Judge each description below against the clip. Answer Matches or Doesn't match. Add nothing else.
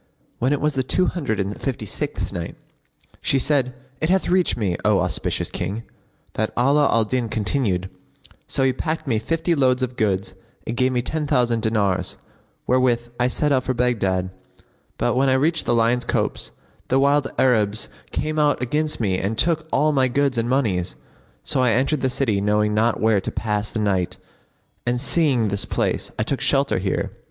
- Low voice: Matches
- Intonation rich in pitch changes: Doesn't match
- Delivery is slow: Doesn't match